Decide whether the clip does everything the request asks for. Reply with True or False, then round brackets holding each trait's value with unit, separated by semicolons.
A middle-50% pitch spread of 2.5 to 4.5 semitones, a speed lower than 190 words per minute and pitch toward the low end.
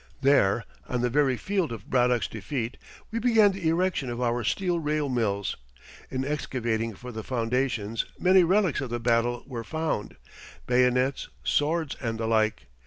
False (5.0 semitones; 160 wpm; 125 Hz)